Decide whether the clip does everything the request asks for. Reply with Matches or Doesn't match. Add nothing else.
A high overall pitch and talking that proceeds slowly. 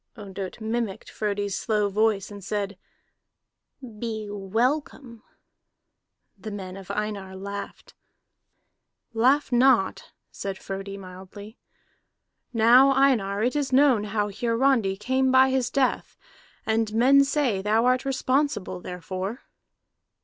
Matches